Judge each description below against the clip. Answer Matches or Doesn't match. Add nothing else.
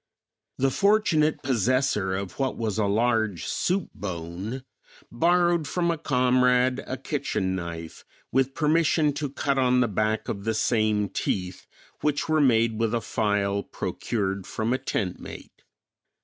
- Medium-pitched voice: Doesn't match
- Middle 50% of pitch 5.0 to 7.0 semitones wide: Matches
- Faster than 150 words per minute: Doesn't match